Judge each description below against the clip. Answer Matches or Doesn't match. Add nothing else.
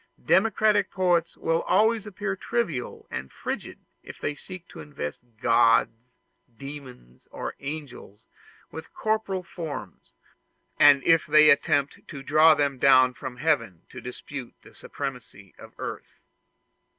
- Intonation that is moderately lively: Doesn't match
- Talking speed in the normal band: Doesn't match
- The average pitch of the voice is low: Doesn't match